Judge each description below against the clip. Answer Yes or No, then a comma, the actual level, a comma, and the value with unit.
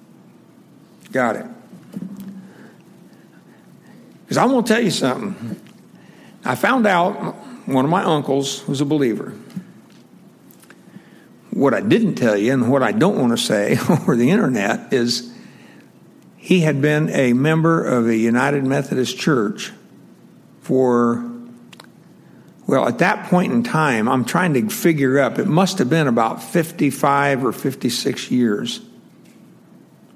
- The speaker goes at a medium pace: No, slow, 130 wpm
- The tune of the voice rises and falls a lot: Yes, wide, 6.6 semitones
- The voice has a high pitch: No, medium, 155 Hz